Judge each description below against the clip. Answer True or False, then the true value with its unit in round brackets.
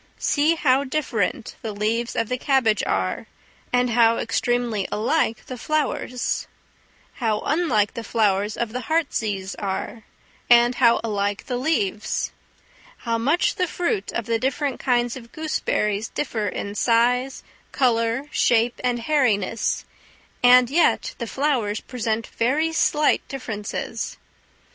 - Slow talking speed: True (130 wpm)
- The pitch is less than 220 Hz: False (235 Hz)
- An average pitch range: True (3.3 semitones)